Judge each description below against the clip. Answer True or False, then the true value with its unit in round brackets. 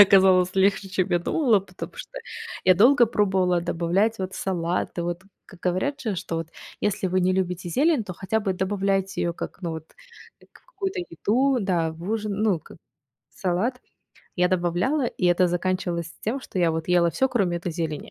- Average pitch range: True (3.1 semitones)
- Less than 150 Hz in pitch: False (185 Hz)